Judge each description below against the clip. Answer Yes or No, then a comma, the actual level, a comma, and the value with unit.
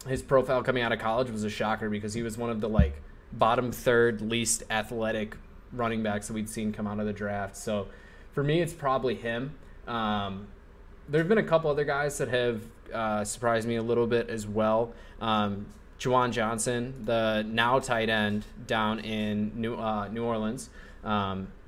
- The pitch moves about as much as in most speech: No, narrow, 2.1 semitones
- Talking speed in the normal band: Yes, average, 185 wpm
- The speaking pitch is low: Yes, low, 110 Hz